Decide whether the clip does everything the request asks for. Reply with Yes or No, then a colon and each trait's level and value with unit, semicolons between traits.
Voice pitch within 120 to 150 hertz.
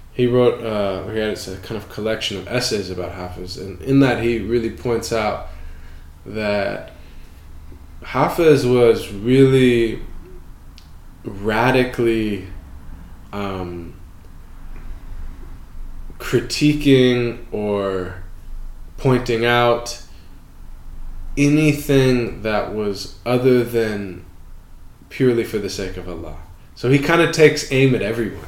No: low, 105 Hz